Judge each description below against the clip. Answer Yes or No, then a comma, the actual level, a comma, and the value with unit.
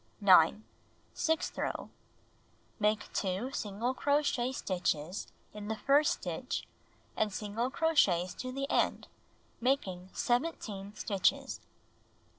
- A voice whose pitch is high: Yes, high, 215 Hz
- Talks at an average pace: No, slow, 100 wpm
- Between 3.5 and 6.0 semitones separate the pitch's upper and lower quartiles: Yes, average, 5.3 semitones